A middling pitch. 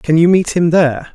Yes: medium, 165 Hz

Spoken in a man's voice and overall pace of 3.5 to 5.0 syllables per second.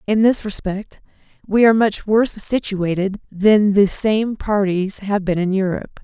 No: female; 4.5 syllables/s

